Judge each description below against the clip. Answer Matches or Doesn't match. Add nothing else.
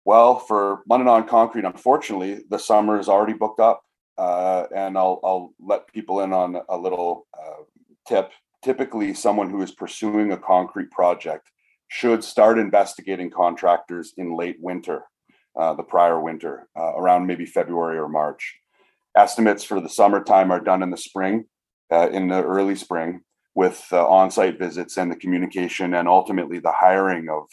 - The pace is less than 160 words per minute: Doesn't match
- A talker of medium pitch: Doesn't match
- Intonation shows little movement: Matches